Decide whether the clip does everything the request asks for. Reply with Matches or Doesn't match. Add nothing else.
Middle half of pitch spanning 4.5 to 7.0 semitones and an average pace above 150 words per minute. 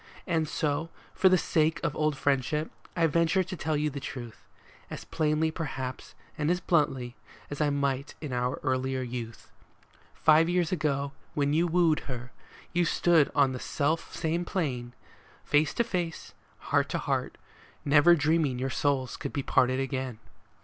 Doesn't match